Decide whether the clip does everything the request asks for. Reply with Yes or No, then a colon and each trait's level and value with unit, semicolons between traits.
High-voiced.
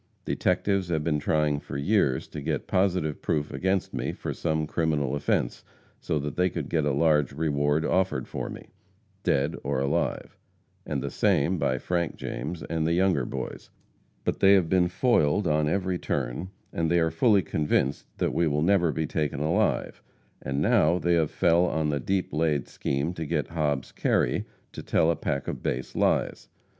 No: very low, 80 Hz